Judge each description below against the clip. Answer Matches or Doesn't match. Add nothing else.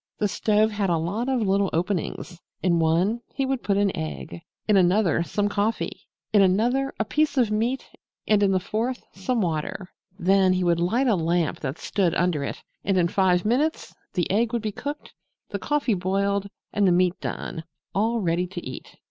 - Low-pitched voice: Doesn't match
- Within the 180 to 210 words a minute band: Matches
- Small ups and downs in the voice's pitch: Doesn't match